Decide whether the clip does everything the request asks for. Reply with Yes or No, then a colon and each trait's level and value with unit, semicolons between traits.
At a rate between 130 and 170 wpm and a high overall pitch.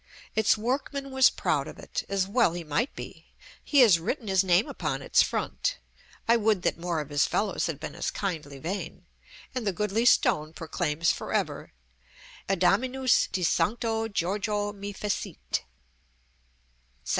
Yes: average, 155 wpm; high, 200 Hz